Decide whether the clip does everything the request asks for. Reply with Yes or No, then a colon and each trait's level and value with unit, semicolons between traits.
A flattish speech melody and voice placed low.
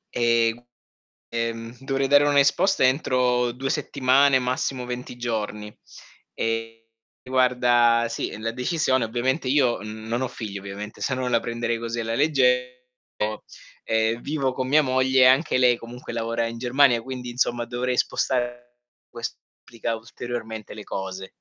Yes: narrow, 2.0 semitones; low, 120 Hz